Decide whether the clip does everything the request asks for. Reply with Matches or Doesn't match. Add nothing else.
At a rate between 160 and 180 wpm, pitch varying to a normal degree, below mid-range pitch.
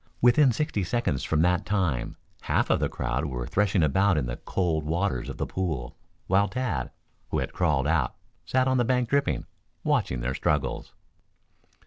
Doesn't match